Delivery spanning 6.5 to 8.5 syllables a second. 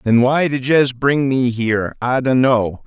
No: 4.1 syllables/s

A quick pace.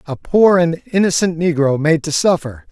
No: average, 175 wpm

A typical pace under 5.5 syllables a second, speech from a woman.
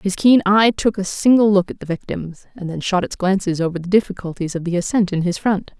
No: 5.8 syllables/s; female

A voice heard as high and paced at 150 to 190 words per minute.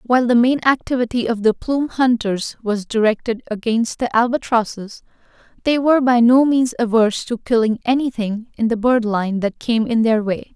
Yes: high, 235 Hz; average, 175 wpm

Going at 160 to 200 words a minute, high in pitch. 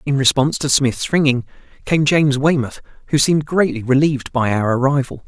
No: average, 170 wpm; medium, 140 Hz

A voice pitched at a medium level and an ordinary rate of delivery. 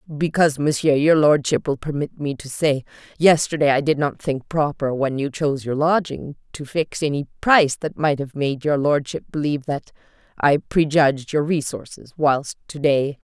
Yes: medium, 145 Hz; average, 175 wpm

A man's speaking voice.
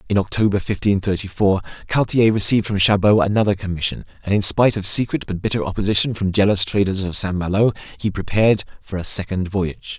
Yes: male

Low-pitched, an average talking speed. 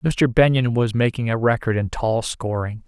Yes: low, 120 Hz; average, 190 wpm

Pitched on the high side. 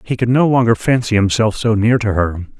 No: low, 110 Hz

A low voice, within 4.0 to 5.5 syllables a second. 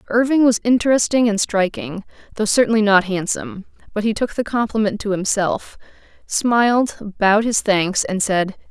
No: high, 215 Hz; 5.0 syllables/s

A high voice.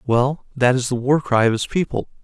No: low, 130 Hz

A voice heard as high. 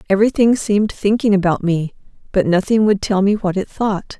Yes: high, 200 Hz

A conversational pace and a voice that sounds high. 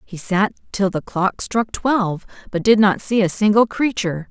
Yes: average, 195 wpm; high, 205 Hz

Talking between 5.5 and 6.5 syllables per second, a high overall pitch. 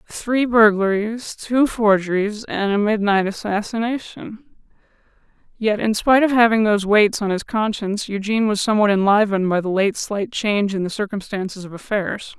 No: 5.3 syllables/s; high, 210 Hz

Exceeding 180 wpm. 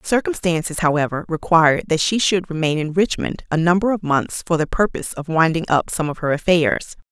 Yes: average, 195 wpm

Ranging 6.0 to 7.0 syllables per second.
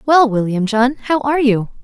No: 5.5 syllables/s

